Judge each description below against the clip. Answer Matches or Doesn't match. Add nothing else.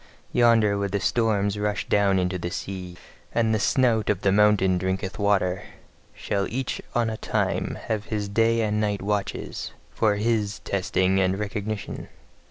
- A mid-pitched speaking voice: Doesn't match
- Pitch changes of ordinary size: Doesn't match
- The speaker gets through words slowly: Doesn't match